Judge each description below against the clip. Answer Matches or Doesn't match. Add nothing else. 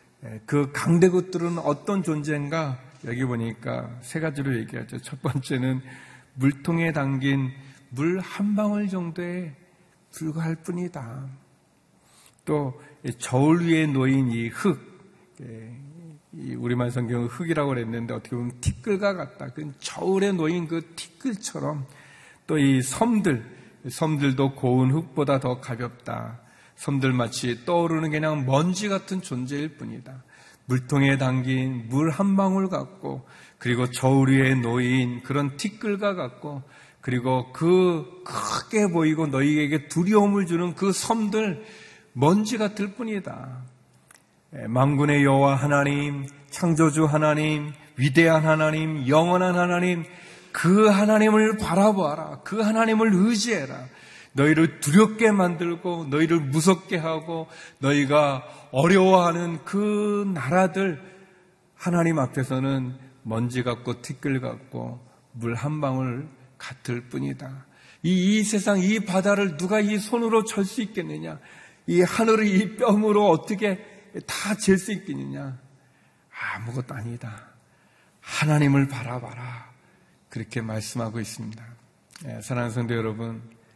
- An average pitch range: Doesn't match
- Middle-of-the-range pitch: Matches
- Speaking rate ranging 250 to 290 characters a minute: Matches